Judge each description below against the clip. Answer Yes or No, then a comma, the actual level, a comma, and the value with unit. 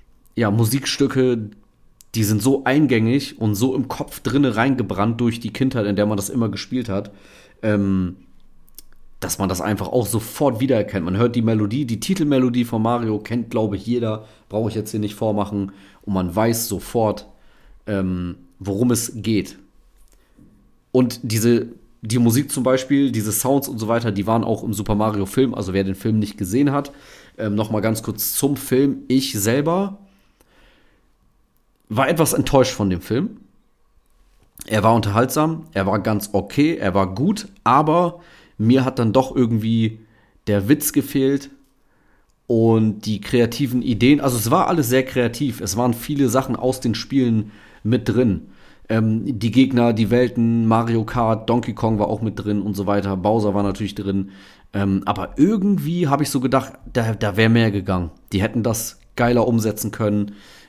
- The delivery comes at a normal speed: Yes, average, 170 wpm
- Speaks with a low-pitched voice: Yes, low, 115 Hz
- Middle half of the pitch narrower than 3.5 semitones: No, average, 3.9 semitones